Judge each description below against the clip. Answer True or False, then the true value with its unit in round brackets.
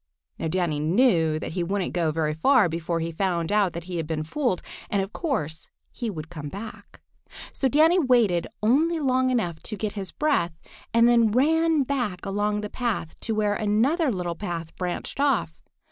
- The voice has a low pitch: False (205 Hz)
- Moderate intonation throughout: False (6.9 semitones)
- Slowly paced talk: False (185 wpm)